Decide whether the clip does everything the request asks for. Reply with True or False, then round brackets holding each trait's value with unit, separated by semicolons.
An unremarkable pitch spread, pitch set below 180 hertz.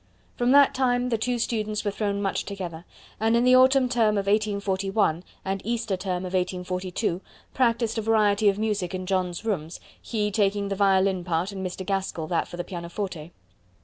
False (3.3 semitones; 200 Hz)